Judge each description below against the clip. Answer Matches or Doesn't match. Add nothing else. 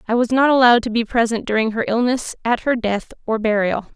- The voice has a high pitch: Matches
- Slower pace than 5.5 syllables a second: Doesn't match